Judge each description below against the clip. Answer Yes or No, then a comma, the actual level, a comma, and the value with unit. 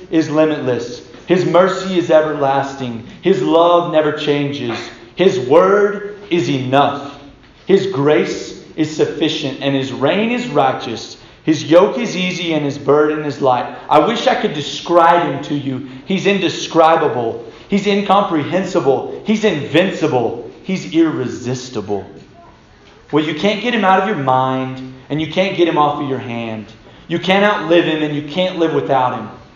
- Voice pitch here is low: No, medium, 155 Hz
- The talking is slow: No, average, 155 wpm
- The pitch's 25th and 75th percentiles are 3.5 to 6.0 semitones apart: Yes, average, 5.1 semitones